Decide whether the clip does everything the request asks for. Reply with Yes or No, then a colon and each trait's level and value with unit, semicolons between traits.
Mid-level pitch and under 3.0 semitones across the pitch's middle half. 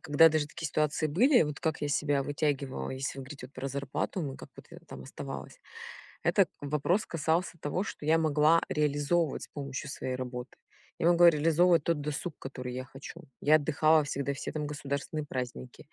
Yes: medium, 145 Hz; narrow, 2.6 semitones